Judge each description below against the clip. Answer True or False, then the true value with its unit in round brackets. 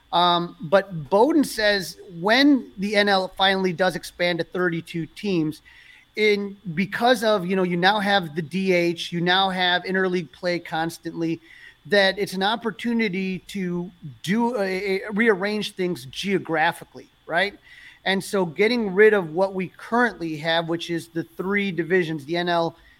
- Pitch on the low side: False (185 Hz)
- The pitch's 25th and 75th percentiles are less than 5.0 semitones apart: True (2.9 semitones)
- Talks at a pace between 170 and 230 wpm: False (150 wpm)